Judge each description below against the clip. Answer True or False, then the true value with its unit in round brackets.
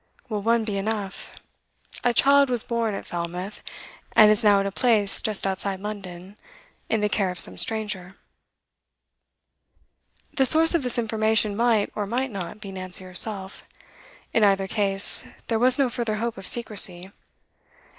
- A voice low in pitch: False (210 Hz)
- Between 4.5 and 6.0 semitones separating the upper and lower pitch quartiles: False (3.0 semitones)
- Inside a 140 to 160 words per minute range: True (155 wpm)